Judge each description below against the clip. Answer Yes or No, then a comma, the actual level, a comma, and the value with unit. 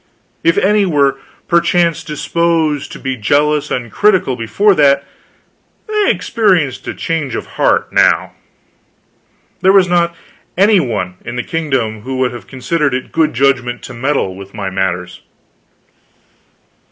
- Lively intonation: Yes, wide, 5.7 semitones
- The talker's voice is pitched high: No, medium, 140 Hz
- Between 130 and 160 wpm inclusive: Yes, average, 140 wpm